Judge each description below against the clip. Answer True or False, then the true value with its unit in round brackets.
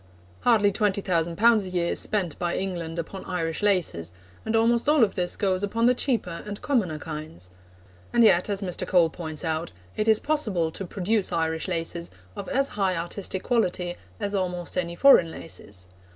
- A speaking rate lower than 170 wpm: False (180 wpm)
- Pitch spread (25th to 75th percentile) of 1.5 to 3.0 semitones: False (4.0 semitones)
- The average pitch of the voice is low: False (185 Hz)